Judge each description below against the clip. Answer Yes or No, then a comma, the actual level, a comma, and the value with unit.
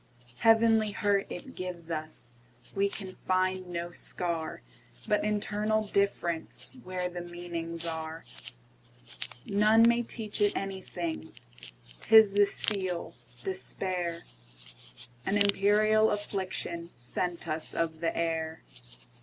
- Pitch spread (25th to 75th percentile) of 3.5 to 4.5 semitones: Yes, average, 4.2 semitones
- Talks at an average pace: No, slow, 85 wpm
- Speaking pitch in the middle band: Yes, medium, 175 Hz